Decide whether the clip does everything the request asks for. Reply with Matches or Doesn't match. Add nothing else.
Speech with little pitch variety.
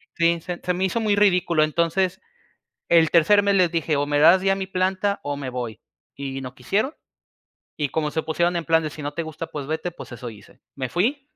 Doesn't match